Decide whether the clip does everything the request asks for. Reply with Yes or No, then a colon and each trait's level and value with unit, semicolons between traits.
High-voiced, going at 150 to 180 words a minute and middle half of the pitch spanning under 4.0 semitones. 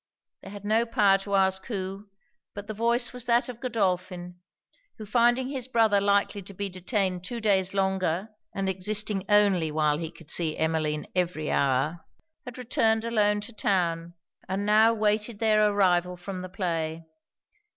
Yes: high, 195 Hz; average, 160 wpm; average, 3.4 semitones